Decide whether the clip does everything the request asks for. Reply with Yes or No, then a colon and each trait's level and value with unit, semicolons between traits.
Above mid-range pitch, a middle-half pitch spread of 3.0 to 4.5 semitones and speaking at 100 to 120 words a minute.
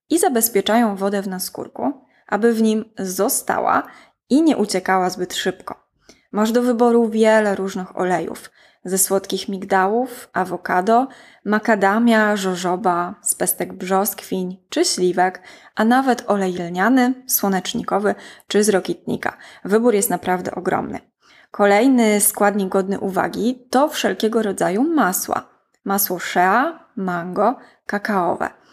Yes: high, 205 Hz; average, 3.9 semitones; average, 115 wpm